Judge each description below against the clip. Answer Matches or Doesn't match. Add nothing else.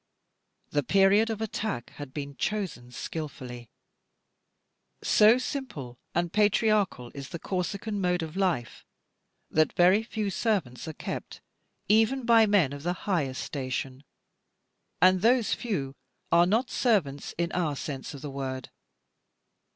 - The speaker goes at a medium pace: Doesn't match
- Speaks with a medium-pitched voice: Matches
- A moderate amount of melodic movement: Doesn't match